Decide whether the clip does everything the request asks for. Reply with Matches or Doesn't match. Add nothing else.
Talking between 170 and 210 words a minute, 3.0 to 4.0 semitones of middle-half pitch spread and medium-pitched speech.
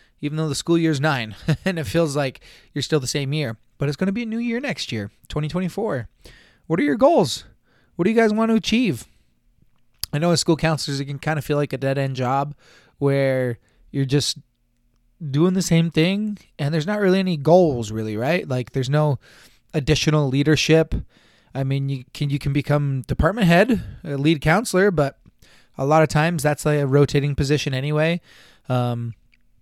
Matches